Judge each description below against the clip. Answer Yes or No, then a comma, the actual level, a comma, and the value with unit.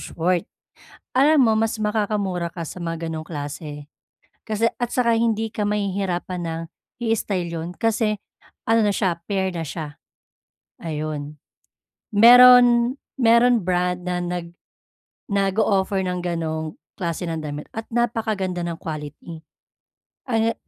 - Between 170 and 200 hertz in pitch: Yes, high, 190 Hz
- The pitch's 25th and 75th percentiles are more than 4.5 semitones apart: Yes, average, 5.1 semitones